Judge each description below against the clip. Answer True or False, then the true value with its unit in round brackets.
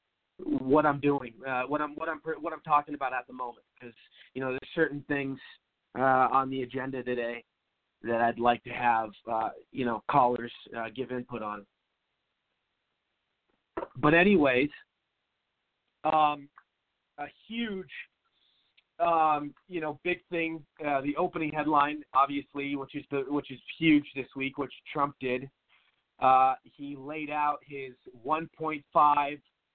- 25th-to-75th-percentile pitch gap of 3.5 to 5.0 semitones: False (3.1 semitones)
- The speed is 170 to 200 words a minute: False (145 wpm)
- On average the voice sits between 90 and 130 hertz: False (140 Hz)